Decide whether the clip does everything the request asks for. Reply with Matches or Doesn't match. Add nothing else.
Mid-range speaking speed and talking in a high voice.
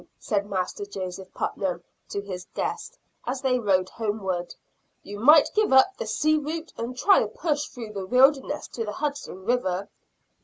Matches